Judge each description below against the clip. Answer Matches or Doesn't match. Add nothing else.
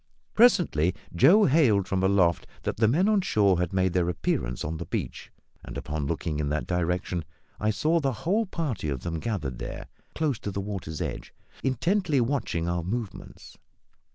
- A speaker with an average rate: Matches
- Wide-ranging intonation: Matches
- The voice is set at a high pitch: Doesn't match